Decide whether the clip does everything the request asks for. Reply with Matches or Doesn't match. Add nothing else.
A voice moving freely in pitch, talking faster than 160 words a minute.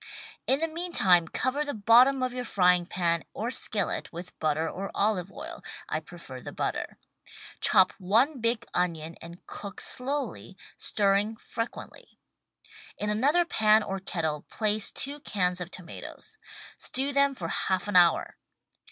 Doesn't match